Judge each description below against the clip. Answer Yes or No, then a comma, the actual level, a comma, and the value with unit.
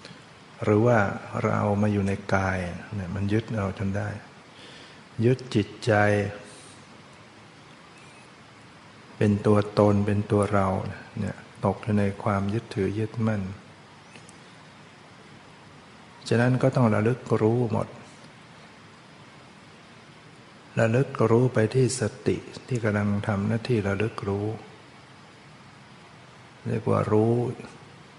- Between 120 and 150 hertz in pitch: No, low, 105 Hz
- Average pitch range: No, narrow, 2.3 semitones